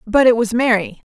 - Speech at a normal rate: No, fast, 215 wpm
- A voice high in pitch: Yes, high, 230 Hz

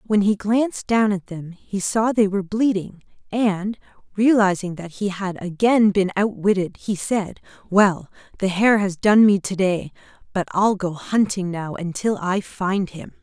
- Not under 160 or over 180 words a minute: Yes, average, 170 wpm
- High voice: Yes, high, 195 Hz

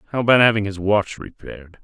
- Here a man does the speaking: Yes, male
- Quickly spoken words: No, average, 195 wpm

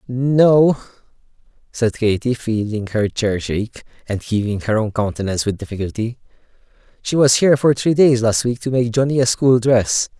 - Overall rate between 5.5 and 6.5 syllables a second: No, 5.0 syllables/s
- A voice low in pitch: Yes, low, 115 Hz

